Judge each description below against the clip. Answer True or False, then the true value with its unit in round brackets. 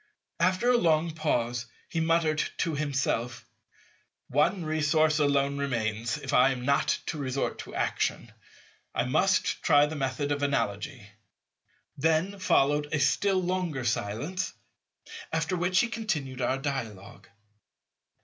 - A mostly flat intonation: False (4.1 semitones)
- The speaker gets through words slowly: True (130 wpm)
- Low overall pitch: False (145 Hz)